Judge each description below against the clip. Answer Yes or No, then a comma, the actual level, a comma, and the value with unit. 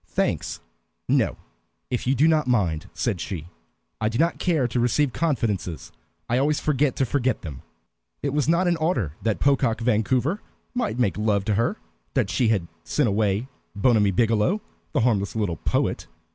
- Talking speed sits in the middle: Yes, average, 170 wpm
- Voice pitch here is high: No, low, 120 Hz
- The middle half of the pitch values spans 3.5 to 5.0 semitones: No, wide, 5.6 semitones